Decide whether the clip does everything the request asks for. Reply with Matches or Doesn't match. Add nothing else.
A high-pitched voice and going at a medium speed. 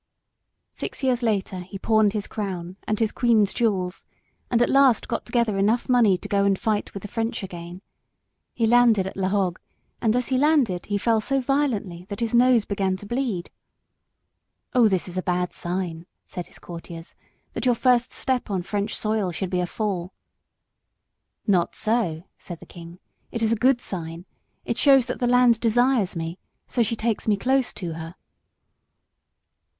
Matches